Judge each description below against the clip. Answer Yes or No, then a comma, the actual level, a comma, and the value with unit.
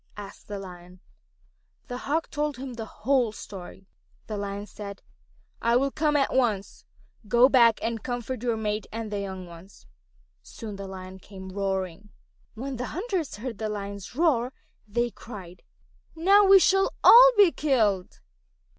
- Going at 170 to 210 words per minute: No, average, 155 wpm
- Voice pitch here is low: No, high, 225 Hz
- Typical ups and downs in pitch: Yes, average, 5.0 semitones